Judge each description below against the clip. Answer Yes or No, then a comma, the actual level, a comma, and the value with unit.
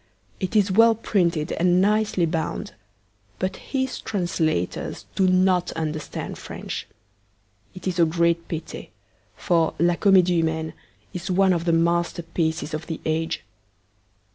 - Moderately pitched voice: Yes, medium, 175 Hz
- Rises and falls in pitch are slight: Yes, narrow, 2.3 semitones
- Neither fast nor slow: No, slow, 130 wpm